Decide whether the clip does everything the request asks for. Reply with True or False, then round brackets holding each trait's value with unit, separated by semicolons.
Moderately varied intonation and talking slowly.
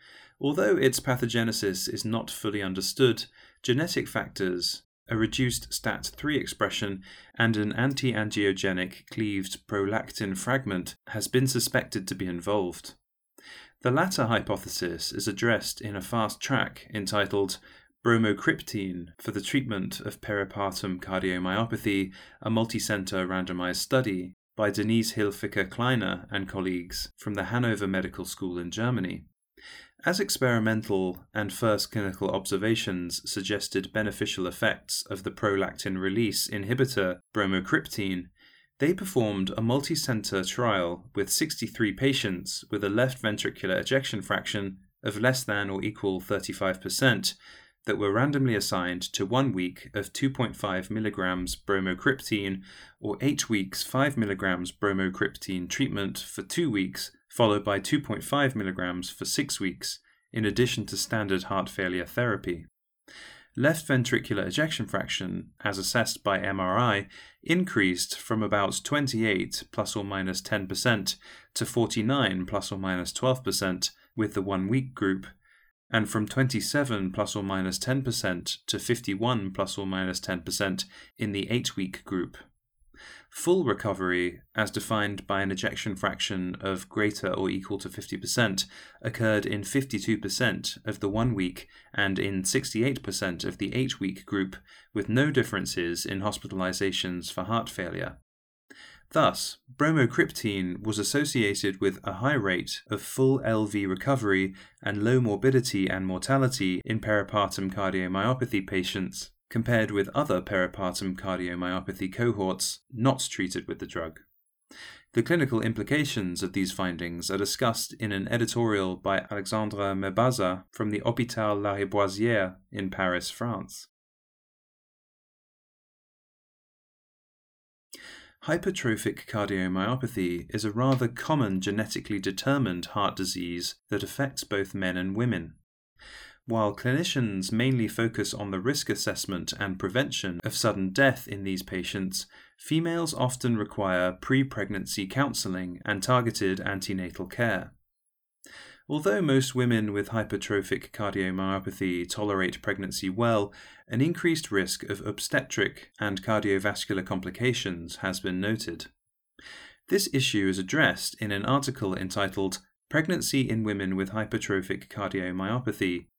True (3.6 semitones; 125 wpm)